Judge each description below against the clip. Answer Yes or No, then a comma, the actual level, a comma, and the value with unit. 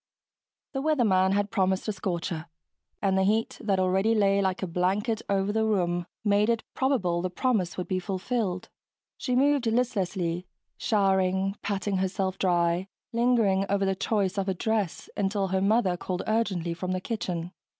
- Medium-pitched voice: No, high, 195 Hz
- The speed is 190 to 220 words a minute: No, average, 165 wpm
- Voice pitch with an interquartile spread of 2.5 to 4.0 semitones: Yes, average, 2.8 semitones